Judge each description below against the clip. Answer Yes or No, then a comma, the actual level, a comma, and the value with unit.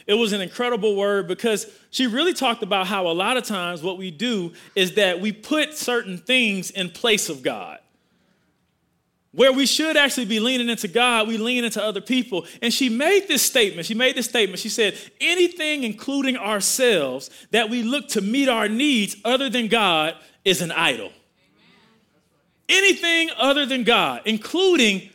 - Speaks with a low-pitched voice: No, high, 230 Hz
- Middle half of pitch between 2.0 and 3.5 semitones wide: No, average, 4.3 semitones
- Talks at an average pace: Yes, average, 175 wpm